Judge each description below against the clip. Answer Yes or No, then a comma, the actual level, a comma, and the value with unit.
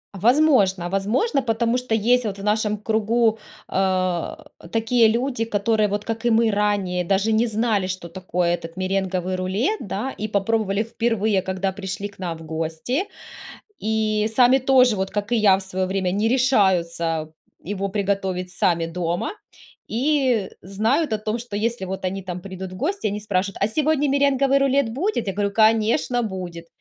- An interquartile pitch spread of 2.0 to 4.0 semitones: Yes, average, 3.7 semitones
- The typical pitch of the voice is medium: No, high, 210 Hz